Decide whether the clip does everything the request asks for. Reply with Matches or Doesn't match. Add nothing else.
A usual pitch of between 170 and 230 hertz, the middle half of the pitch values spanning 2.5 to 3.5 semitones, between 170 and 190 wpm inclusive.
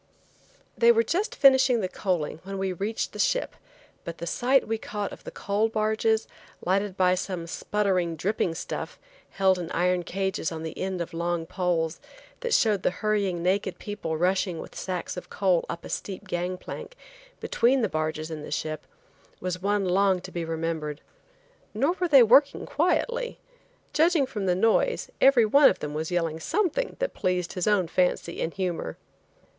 Doesn't match